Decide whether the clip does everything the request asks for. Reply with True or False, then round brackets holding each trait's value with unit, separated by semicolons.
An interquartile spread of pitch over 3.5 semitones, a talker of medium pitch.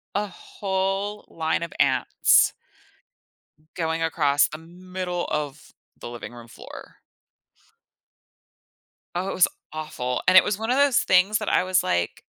True (4.1 semitones; 180 Hz)